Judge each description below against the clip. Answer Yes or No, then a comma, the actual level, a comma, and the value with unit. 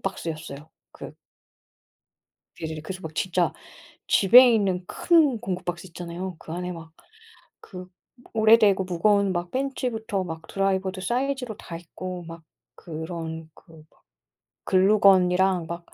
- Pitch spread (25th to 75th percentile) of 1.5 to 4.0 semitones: Yes, average, 3.2 semitones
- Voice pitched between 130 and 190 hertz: Yes, medium, 185 Hz